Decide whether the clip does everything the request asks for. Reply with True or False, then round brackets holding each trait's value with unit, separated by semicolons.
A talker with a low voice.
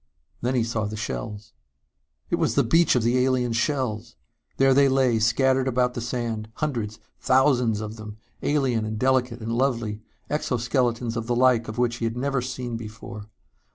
True (120 Hz)